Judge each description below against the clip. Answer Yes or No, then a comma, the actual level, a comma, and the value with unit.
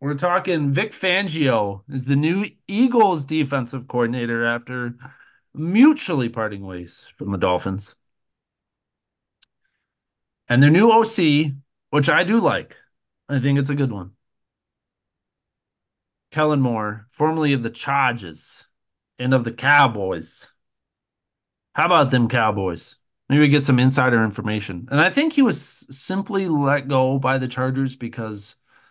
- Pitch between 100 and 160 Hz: Yes, low, 135 Hz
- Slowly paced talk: Yes, slow, 130 wpm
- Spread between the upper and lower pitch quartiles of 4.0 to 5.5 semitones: Yes, average, 4.5 semitones